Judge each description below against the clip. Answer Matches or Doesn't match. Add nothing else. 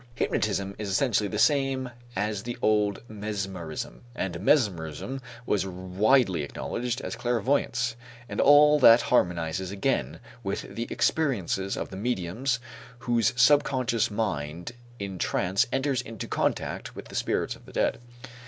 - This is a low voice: Matches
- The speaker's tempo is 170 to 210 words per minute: Doesn't match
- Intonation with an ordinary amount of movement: Matches